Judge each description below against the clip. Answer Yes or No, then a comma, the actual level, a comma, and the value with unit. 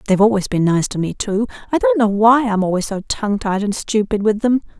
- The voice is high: Yes, high, 215 Hz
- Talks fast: Yes, fast, 250 wpm